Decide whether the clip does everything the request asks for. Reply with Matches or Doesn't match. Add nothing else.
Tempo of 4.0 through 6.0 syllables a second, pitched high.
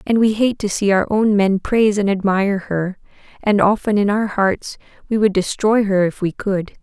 Matches